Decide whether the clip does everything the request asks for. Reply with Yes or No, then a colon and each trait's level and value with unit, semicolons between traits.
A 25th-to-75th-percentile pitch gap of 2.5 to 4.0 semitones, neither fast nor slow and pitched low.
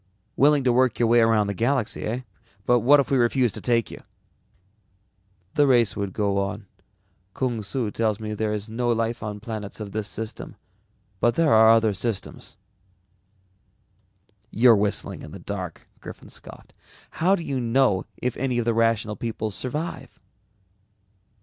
Yes: average, 2.8 semitones; average, 160 wpm; low, 115 Hz